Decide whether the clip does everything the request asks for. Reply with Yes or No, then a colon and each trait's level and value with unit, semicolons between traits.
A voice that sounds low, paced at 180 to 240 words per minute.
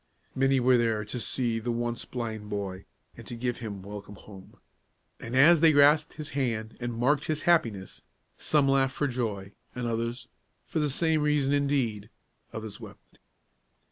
No: low, 120 Hz; average, 160 wpm